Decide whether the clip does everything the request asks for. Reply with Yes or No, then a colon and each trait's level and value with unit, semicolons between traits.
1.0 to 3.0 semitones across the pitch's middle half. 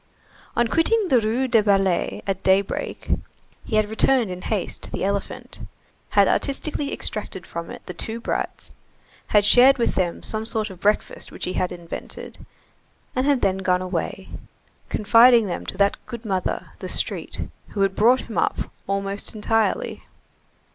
No: average, 3.6 semitones